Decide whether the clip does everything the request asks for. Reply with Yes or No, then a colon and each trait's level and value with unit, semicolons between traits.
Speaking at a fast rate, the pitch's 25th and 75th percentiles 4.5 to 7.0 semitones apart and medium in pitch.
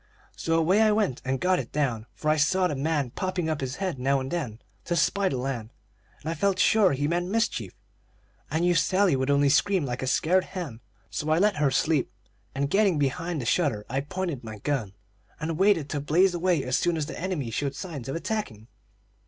Yes: fast, 215 wpm; average, 5.2 semitones; medium, 155 Hz